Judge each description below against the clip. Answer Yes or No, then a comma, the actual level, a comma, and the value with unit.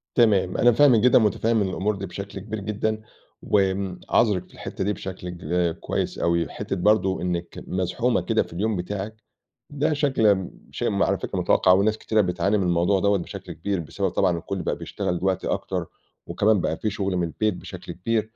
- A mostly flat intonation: No, average, 3.2 semitones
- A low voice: Yes, low, 100 Hz